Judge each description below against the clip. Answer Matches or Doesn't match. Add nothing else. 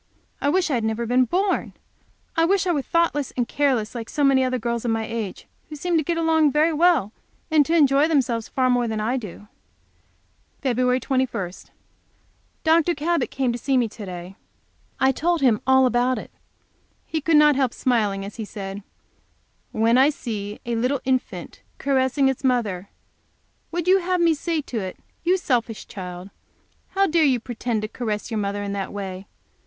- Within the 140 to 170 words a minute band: Doesn't match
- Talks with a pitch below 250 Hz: Doesn't match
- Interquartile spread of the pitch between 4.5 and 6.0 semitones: Matches